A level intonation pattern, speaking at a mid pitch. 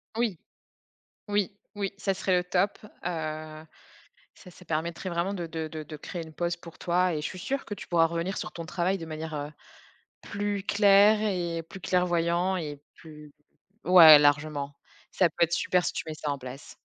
No: average, 3.2 semitones; medium, 170 Hz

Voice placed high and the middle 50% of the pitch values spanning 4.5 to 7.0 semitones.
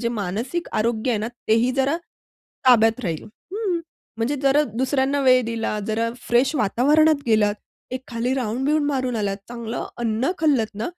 No: high, 245 Hz; average, 3.6 semitones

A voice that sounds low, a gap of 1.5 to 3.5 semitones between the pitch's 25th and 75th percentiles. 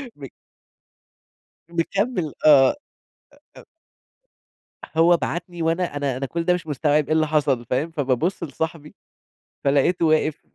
No: medium, 155 Hz; average, 2.9 semitones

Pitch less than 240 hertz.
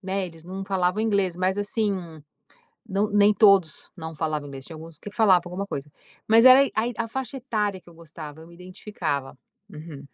Yes: medium, 185 Hz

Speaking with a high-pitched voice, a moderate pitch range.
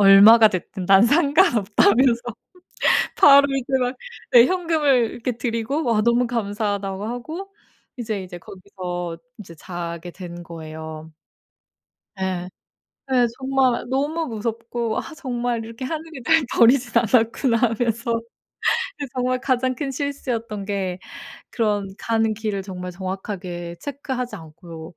Yes: high, 230 Hz; average, 5.0 semitones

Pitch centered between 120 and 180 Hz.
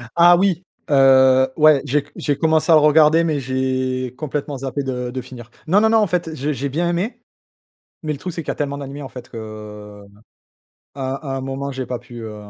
Yes: medium, 140 Hz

